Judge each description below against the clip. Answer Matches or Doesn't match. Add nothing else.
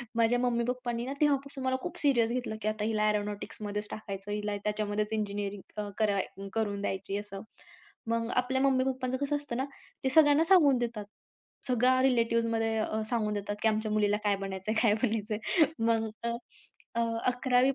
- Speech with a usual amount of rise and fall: Matches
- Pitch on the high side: Matches